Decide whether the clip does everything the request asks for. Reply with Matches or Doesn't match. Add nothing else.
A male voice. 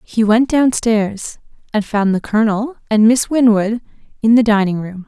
Doesn't match